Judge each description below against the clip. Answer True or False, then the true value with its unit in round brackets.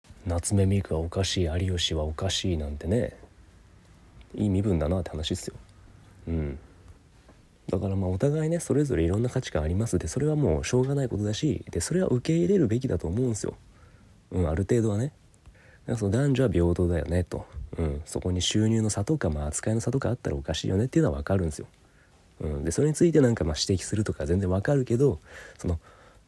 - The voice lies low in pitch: True (95 Hz)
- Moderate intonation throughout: False (5.7 semitones)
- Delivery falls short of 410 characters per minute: False (420 characters per minute)